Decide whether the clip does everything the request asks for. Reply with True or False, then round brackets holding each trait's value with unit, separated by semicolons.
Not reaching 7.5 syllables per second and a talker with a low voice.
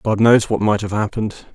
True (5.5 syllables/s; 105 Hz)